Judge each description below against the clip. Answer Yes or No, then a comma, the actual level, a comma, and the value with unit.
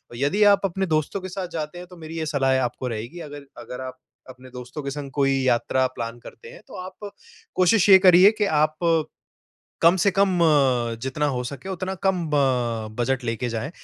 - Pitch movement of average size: No, wide, 6.1 semitones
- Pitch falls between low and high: Yes, medium, 150 Hz